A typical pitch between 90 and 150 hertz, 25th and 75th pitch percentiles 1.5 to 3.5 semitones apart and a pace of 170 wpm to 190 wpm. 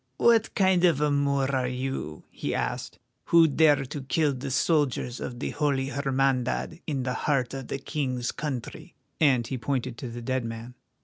Yes: low, 135 Hz; average, 2.7 semitones; average, 180 wpm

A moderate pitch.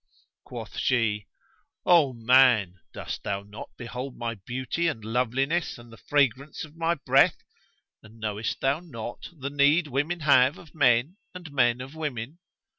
No: low, 130 Hz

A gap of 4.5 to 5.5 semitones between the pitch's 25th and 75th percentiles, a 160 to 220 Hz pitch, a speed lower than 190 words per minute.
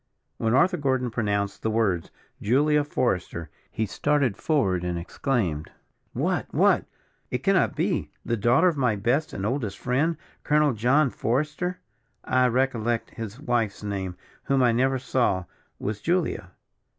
No: average, 5.2 semitones; low, 120 Hz; average, 140 wpm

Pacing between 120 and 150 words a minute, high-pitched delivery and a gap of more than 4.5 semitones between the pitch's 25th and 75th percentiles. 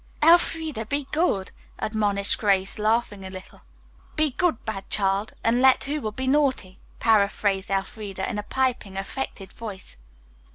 Yes: average, 140 wpm; high, 215 Hz; average, 5.2 semitones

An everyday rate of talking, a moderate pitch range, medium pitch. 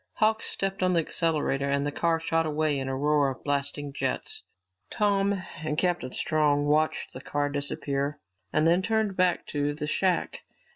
Yes: average, 175 wpm; average, 4.1 semitones; medium, 150 Hz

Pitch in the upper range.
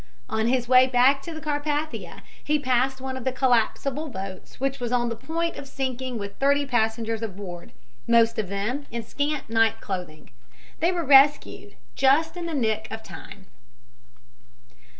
Yes: very high, 255 Hz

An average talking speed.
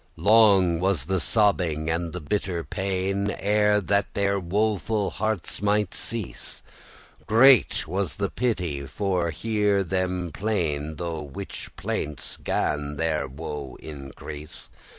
No: slow, 130 wpm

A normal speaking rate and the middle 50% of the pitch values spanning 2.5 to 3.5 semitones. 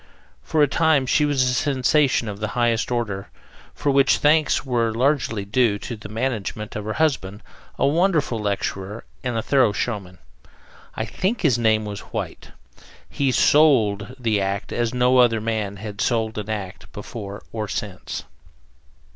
No: average, 160 wpm; average, 4.3 semitones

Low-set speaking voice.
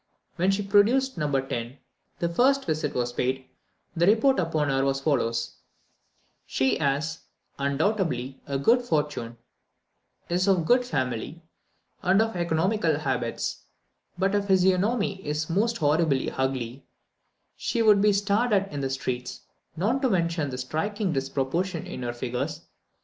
No: medium, 160 Hz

